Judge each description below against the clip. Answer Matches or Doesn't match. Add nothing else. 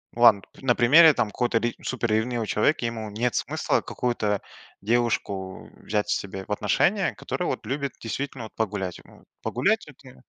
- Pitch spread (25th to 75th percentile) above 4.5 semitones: Doesn't match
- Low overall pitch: Matches